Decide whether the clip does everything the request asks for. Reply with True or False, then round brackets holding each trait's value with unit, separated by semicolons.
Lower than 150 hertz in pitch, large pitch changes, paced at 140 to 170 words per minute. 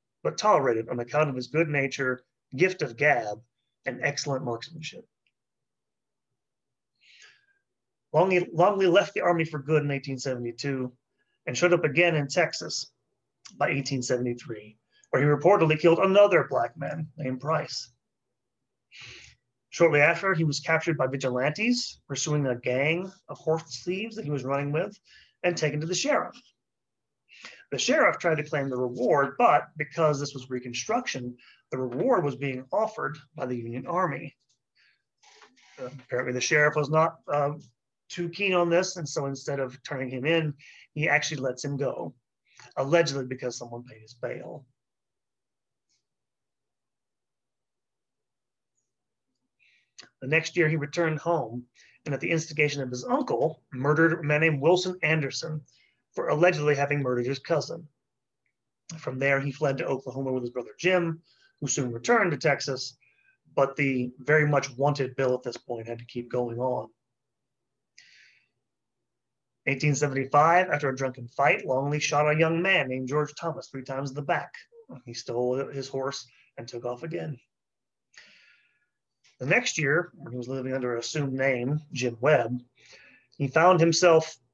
False (140 Hz; 4.2 semitones; 150 wpm)